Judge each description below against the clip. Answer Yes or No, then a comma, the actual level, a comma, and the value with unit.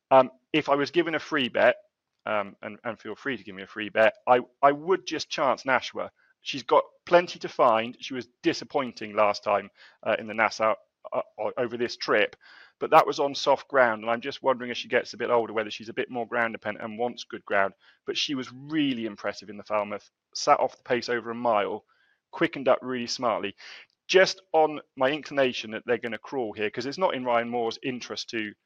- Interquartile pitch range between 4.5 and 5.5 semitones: Yes, average, 4.9 semitones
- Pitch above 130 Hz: No, low, 125 Hz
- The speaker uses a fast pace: Yes, fast, 225 wpm